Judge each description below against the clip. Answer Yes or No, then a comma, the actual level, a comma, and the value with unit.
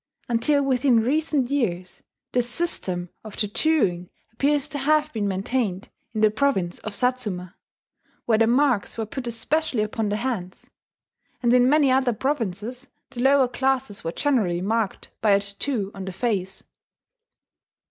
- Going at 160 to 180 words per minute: No, average, 145 wpm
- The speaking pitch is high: Yes, high, 235 Hz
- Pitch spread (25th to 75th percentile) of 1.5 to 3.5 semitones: No, average, 5.0 semitones